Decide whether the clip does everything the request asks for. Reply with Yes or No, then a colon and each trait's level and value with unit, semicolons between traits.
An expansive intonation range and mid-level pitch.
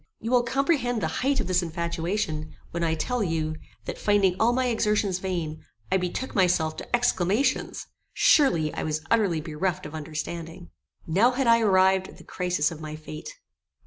Yes: wide, 5.9 semitones; medium, 180 Hz